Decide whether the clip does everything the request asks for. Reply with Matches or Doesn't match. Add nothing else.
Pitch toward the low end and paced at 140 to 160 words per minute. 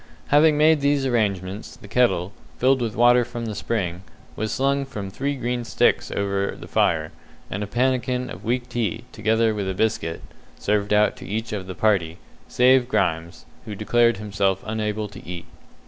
Doesn't match